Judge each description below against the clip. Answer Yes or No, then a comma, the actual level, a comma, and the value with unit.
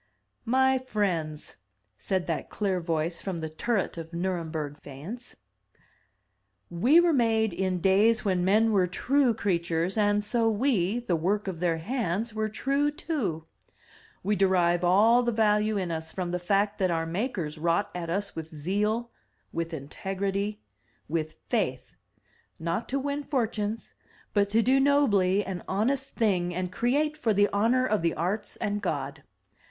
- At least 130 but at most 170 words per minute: Yes, average, 160 wpm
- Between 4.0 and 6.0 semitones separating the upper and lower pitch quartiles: Yes, average, 4.8 semitones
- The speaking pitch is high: Yes, high, 200 Hz